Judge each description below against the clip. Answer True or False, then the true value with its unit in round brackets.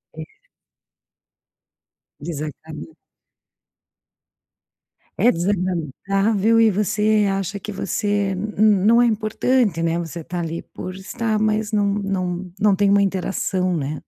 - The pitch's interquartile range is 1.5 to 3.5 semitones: True (3.1 semitones)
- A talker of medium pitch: False (195 Hz)